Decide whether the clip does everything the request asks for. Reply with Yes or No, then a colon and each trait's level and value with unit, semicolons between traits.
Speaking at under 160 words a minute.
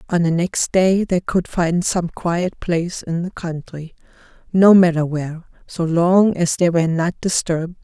No: average, 170 wpm